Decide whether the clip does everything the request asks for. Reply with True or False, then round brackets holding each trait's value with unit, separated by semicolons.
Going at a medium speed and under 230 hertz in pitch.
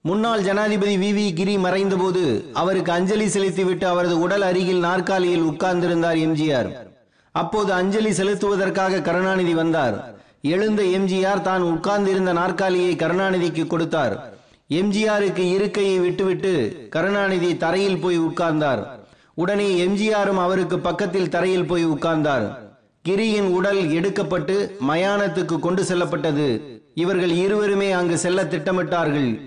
True (105 wpm; 185 Hz)